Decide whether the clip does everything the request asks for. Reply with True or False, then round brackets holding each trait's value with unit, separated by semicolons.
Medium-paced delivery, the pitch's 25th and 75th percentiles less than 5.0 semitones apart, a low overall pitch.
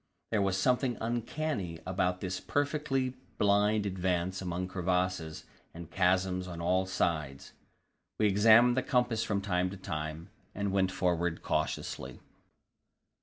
False (125 wpm; 3.3 semitones; 95 Hz)